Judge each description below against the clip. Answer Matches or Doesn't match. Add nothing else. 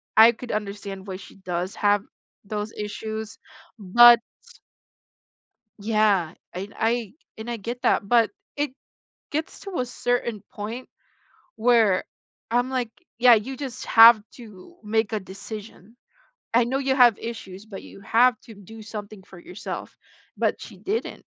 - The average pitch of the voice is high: Matches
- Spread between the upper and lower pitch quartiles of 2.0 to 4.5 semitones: Matches